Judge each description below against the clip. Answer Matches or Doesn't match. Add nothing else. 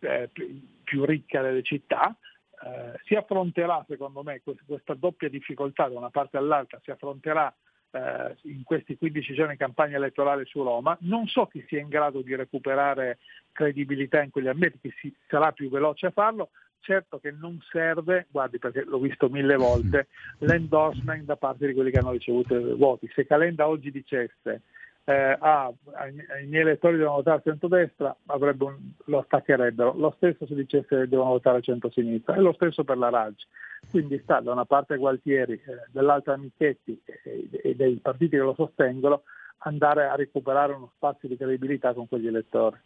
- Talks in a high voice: Doesn't match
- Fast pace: Matches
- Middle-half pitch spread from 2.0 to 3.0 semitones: Matches